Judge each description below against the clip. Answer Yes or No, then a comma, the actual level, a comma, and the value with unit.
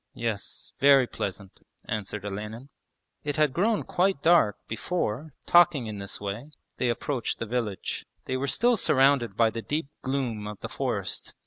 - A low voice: Yes, low, 125 Hz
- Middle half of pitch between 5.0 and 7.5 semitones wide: Yes, wide, 5.5 semitones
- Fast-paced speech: No, average, 155 wpm